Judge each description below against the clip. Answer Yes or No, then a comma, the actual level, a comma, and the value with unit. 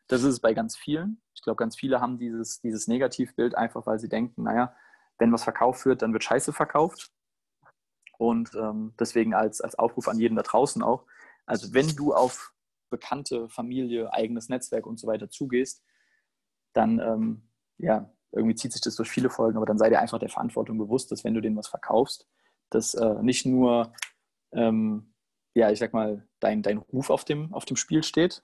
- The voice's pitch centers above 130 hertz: No, low, 115 Hz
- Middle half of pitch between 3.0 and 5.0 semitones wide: No, narrow, 2.5 semitones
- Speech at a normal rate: No, fast, 195 wpm